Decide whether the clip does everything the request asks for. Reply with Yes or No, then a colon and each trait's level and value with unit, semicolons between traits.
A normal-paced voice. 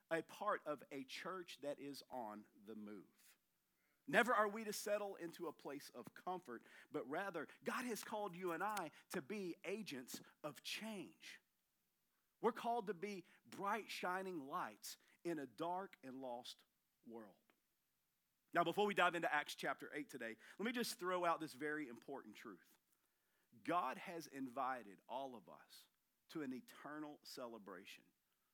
Yes: average, 155 wpm